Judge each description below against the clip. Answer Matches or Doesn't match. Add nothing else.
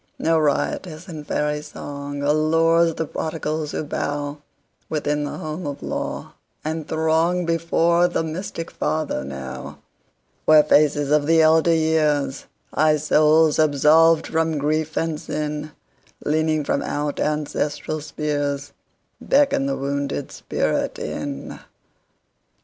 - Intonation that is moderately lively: Doesn't match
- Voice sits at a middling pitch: Matches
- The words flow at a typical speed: Doesn't match